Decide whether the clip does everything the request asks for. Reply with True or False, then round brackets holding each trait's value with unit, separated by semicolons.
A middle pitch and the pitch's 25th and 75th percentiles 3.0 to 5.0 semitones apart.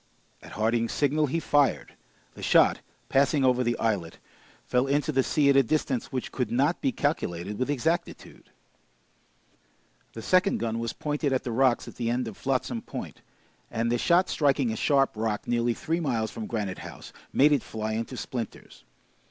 False (125 Hz; 4.1 semitones)